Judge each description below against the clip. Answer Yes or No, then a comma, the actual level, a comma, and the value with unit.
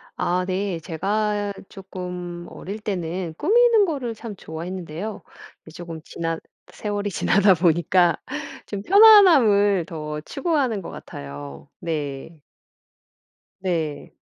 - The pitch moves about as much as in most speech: Yes, average, 4.3 semitones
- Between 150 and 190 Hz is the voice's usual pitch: Yes, medium, 185 Hz